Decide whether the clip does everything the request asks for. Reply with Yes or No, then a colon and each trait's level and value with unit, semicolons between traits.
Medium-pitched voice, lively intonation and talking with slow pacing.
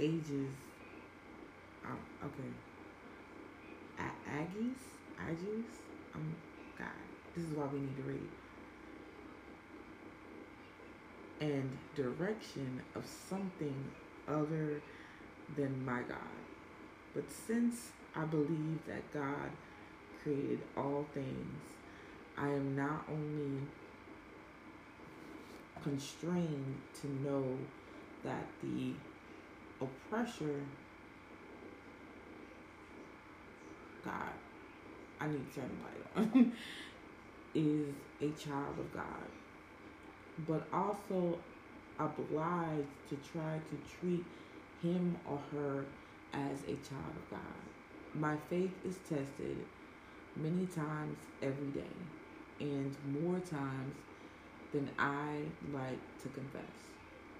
No: medium, 150 Hz; average, 2.8 semitones; slow, 90 wpm